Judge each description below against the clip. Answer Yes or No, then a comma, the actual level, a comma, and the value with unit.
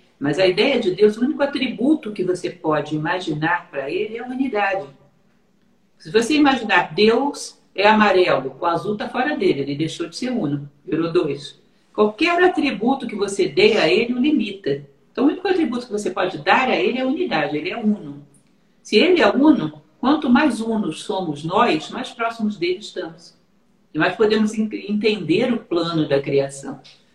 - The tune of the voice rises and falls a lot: Yes, wide, 6.5 semitones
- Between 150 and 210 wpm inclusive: Yes, average, 180 wpm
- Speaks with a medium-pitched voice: No, high, 210 Hz